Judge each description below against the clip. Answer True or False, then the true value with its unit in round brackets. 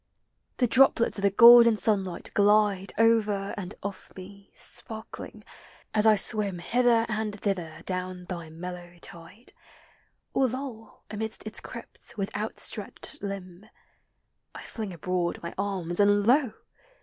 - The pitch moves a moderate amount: True (3.3 semitones)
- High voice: True (205 Hz)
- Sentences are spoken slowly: True (130 wpm)